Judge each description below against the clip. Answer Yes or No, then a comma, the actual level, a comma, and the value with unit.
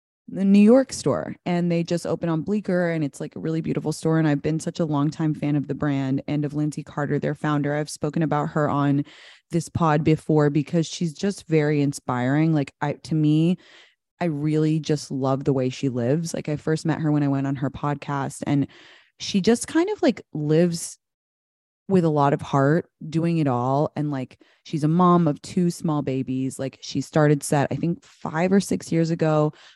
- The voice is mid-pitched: Yes, medium, 150 Hz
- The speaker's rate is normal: No, fast, 210 wpm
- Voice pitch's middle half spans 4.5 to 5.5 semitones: No, average, 2.7 semitones